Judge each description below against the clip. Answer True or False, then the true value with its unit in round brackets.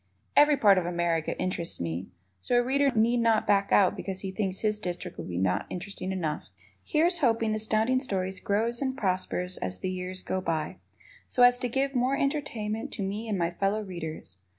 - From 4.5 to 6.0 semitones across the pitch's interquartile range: True (4.9 semitones)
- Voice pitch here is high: True (200 Hz)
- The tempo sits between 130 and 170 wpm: False (195 wpm)